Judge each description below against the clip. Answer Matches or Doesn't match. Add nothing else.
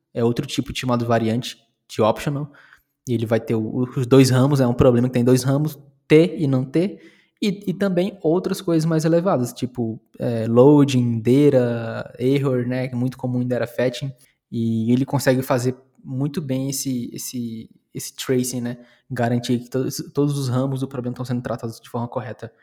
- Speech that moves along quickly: Matches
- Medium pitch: Doesn't match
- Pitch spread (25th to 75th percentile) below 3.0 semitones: Matches